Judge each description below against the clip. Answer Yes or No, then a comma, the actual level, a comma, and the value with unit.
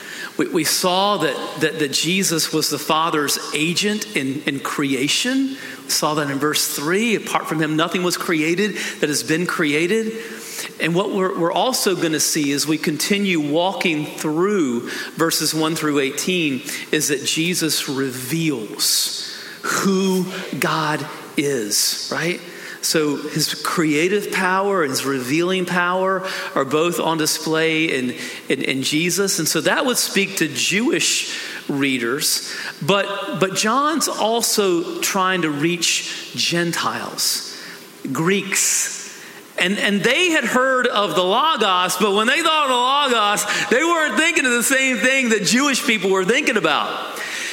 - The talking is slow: No, average, 145 wpm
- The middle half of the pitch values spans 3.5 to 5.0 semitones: No, wide, 5.4 semitones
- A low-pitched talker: No, medium, 180 Hz